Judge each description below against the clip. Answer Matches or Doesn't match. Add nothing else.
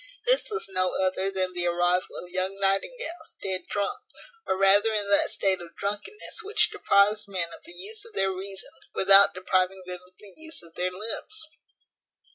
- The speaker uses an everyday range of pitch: Doesn't match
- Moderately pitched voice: Doesn't match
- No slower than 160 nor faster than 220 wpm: Matches